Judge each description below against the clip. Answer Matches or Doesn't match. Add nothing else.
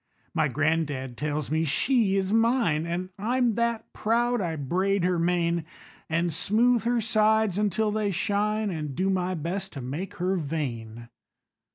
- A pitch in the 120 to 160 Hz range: Doesn't match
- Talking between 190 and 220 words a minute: Doesn't match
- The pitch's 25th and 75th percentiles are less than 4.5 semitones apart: Doesn't match